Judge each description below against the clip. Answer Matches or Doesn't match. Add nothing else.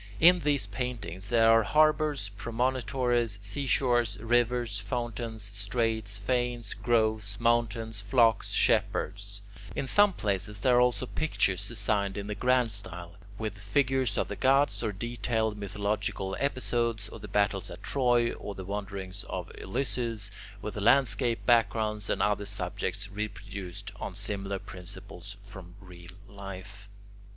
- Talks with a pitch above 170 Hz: Doesn't match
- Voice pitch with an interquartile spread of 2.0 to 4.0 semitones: Matches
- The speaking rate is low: Matches